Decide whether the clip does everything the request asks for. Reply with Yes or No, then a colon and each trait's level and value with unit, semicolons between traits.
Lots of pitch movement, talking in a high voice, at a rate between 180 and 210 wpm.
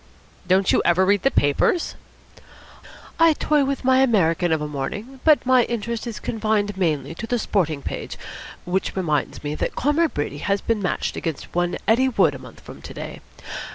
Yes: wide, 7.1 semitones; high, 205 Hz; average, 185 wpm